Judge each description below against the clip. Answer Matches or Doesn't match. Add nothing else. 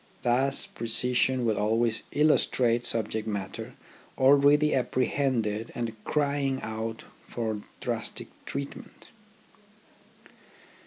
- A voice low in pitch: Matches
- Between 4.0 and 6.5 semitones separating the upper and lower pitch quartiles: Doesn't match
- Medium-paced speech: Doesn't match